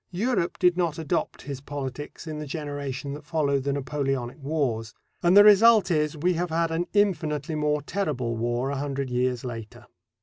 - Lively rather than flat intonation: No, average, 3.7 semitones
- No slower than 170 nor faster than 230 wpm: Yes, average, 175 wpm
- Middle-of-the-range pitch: Yes, medium, 145 Hz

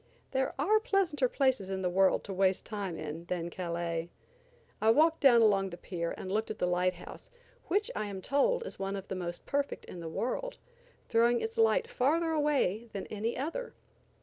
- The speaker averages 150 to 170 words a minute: No, average, 195 wpm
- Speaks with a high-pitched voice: Yes, high, 215 Hz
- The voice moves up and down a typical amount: No, wide, 8.3 semitones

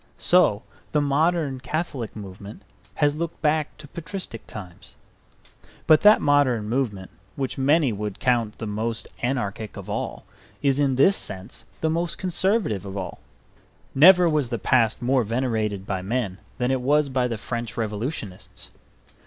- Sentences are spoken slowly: No, average, 150 wpm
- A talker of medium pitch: No, low, 125 Hz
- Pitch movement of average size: No, wide, 5.8 semitones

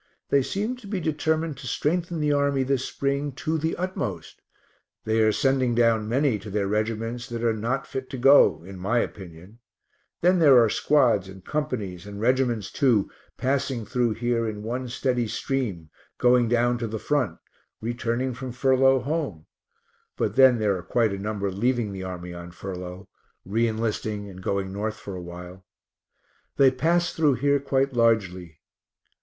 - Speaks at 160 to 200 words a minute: Yes, average, 170 wpm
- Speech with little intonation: No, average, 5.0 semitones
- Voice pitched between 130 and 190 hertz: No, low, 120 Hz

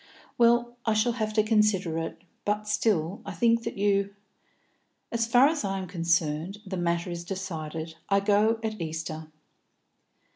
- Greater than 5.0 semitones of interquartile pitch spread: No, average, 4.4 semitones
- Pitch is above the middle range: Yes, high, 200 Hz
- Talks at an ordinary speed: Yes, average, 160 wpm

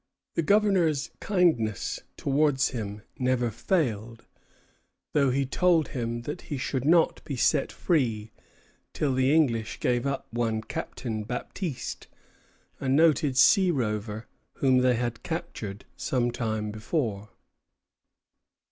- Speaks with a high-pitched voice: No, low, 130 Hz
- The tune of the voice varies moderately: Yes, average, 5.0 semitones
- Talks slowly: Yes, slow, 120 wpm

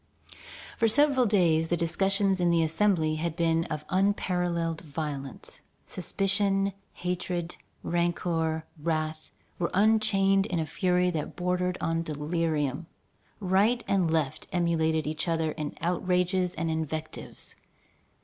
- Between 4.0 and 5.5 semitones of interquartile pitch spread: No, average, 2.9 semitones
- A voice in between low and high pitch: Yes, medium, 170 Hz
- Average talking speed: No, slow, 120 wpm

